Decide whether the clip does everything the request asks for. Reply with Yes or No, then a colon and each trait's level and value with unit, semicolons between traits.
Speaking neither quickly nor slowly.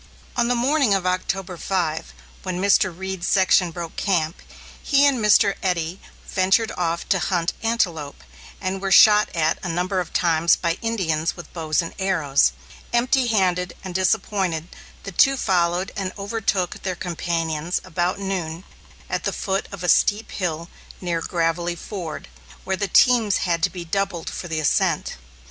Yes: average, 160 wpm